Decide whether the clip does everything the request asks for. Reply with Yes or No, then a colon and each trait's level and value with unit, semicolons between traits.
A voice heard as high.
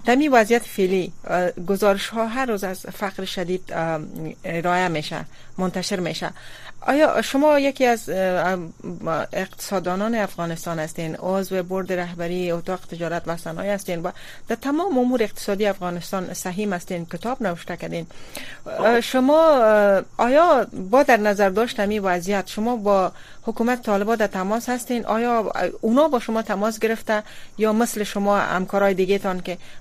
Yes: high, 200 Hz